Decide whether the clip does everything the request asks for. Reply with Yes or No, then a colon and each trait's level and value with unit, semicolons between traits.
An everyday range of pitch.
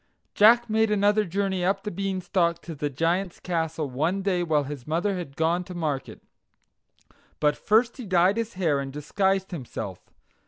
Yes: average, 4.2 semitones